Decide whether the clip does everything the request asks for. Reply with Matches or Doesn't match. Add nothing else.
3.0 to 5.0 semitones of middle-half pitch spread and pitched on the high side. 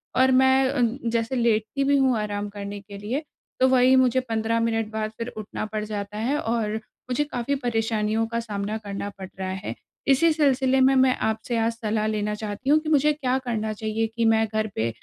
Matches